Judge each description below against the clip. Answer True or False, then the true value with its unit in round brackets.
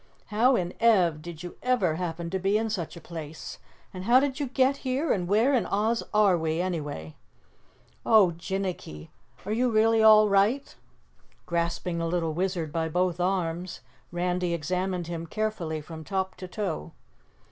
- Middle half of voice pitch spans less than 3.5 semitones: False (4.3 semitones)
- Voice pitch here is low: False (185 Hz)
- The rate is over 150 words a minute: True (160 wpm)